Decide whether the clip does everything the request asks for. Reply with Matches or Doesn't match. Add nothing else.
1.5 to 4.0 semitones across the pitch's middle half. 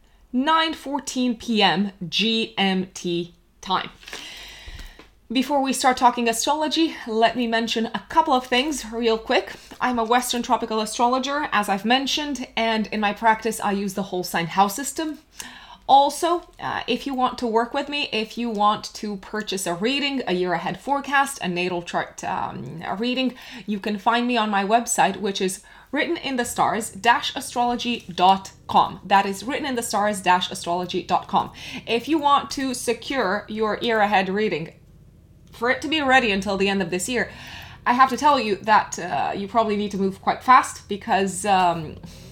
Doesn't match